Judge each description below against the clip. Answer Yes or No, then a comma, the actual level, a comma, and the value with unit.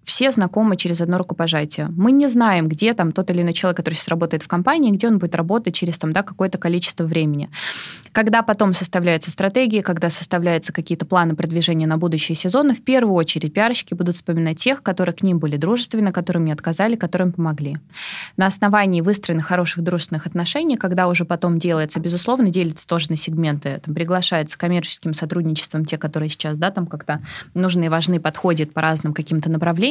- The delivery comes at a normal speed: No, fast, 185 wpm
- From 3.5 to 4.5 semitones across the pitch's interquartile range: No, average, 2.8 semitones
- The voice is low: No, medium, 175 Hz